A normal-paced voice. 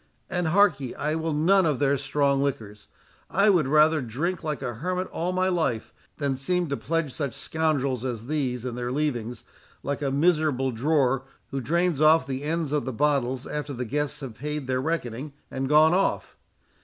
Yes: average, 190 wpm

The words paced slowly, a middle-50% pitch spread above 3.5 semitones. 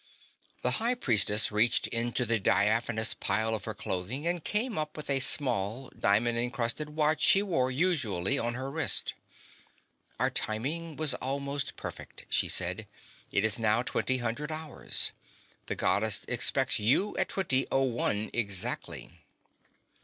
No: average, 145 wpm; wide, 5.4 semitones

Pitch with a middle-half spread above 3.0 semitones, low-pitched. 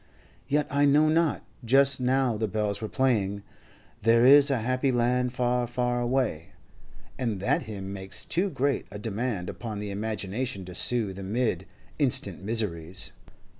Yes: average, 4.1 semitones; low, 120 Hz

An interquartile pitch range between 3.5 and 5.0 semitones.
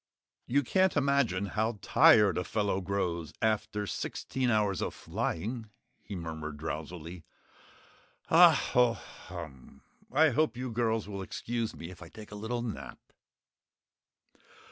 No: wide, 5.4 semitones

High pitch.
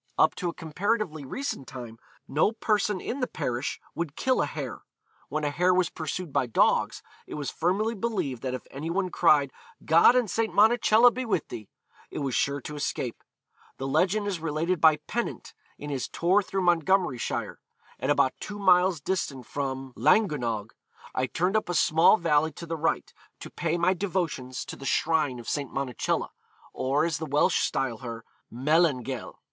No: medium, 160 Hz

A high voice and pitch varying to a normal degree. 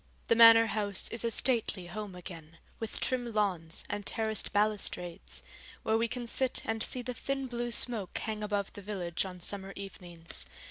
Yes: high, 210 Hz; average, 3.7 semitones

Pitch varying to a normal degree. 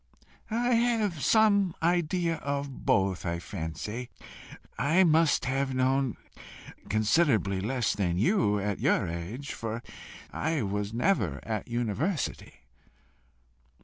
No: wide, 8.2 semitones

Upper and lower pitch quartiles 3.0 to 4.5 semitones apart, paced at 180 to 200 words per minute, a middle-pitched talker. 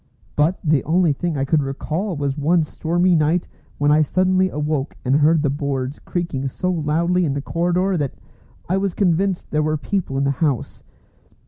Yes: average, 3.6 semitones; average, 185 wpm; medium, 155 Hz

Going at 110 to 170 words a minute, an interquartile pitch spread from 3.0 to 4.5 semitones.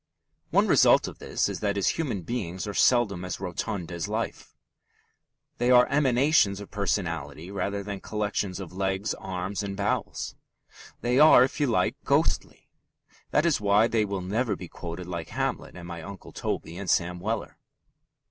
Yes: average, 165 wpm; average, 3.8 semitones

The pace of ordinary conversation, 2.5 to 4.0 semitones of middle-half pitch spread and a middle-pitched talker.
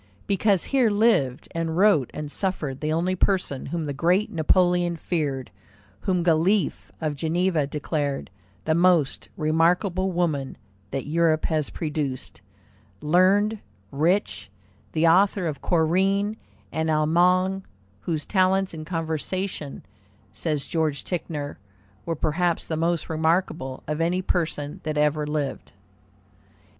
No: slow, 120 wpm; average, 3.2 semitones; medium, 165 Hz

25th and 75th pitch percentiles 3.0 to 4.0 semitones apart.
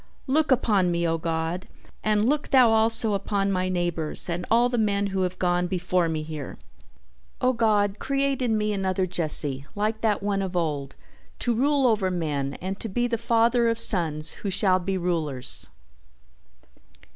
No: average, 4.6 semitones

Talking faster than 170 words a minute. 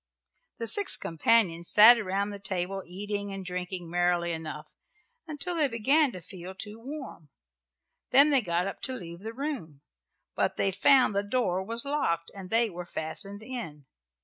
No: average, 165 wpm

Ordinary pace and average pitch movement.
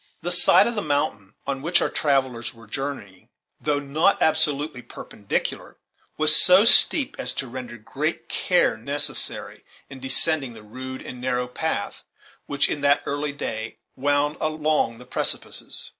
Yes: average, 150 wpm; average, 3.5 semitones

